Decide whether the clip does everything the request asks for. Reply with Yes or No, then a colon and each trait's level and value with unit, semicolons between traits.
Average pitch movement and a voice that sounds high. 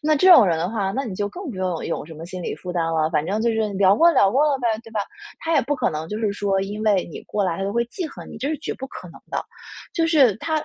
No: wide, 6.6 semitones; high, 205 Hz